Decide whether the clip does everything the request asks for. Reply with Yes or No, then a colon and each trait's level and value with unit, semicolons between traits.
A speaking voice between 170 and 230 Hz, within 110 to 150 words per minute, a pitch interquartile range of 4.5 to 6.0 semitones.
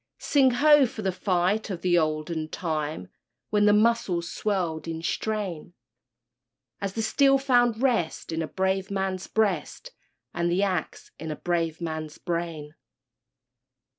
Yes: medium, 185 Hz; average, 140 wpm; average, 4.8 semitones